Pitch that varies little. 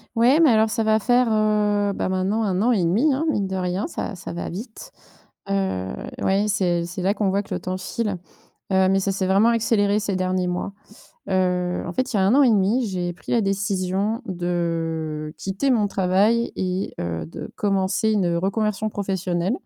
No: average, 3.0 semitones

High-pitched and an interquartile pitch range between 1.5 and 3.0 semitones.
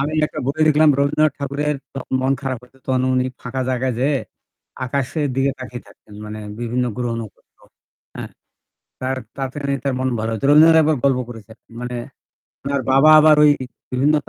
No: low, 135 Hz; narrow, 2.6 semitones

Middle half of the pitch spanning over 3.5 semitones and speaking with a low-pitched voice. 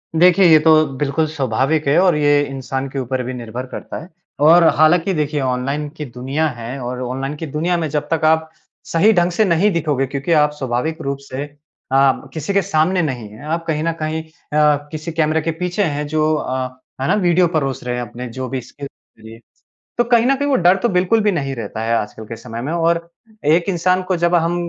No: average, 4.2 semitones; medium, 155 Hz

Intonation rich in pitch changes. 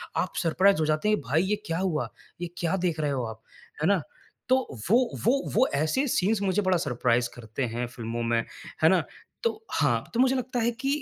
Yes: wide, 7.9 semitones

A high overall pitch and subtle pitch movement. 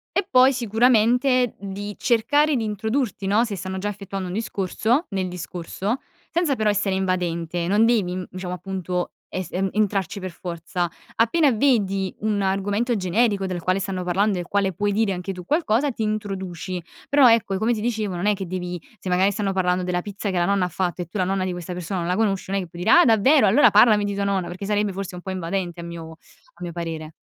No: high, 195 Hz; average, 3.1 semitones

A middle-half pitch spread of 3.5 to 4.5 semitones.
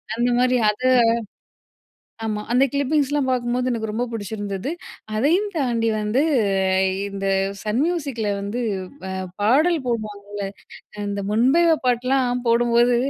Yes: average, 3.9 semitones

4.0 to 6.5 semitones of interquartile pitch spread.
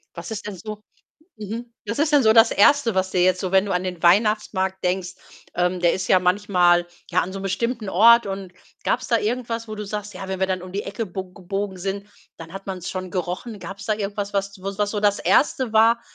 No: average, 2.7 semitones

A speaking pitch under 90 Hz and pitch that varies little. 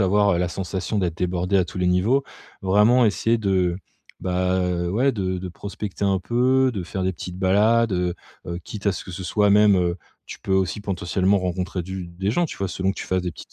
No: very low, 95 Hz; narrow, 2.3 semitones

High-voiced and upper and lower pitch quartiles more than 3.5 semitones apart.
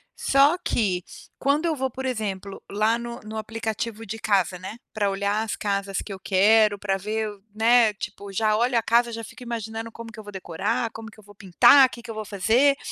No: high, 220 Hz; average, 2.7 semitones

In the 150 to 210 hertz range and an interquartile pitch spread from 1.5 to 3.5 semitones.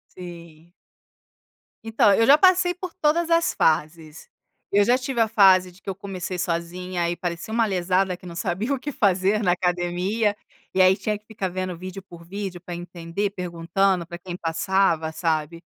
Yes: medium, 185 Hz; average, 3.1 semitones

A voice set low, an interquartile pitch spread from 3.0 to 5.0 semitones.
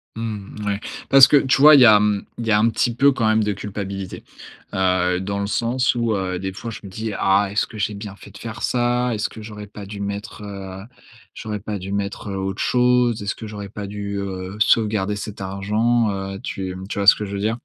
No: low, 105 Hz; narrow, 2.4 semitones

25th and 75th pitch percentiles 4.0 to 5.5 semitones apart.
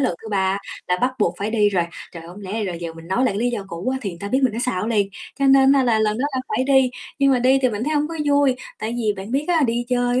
Yes: average, 4.6 semitones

